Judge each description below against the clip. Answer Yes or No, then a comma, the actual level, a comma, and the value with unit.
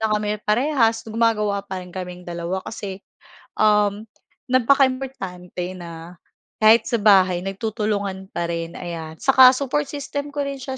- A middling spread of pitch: No, wide, 5.7 semitones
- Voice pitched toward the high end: Yes, high, 210 Hz